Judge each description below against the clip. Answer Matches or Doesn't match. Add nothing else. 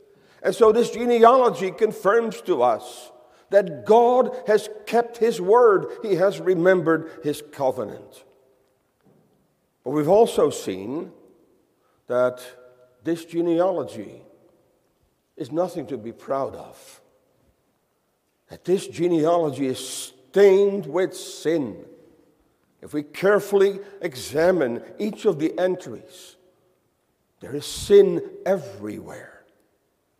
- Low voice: Doesn't match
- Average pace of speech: Doesn't match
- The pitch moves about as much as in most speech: Doesn't match